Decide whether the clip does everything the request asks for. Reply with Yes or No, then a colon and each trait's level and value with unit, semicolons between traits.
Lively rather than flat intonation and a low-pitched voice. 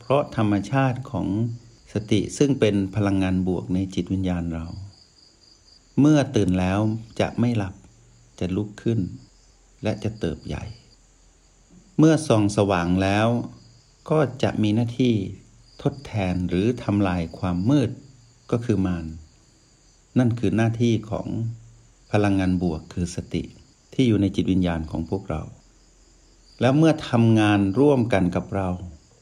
No: average, 4.4 semitones; low, 105 Hz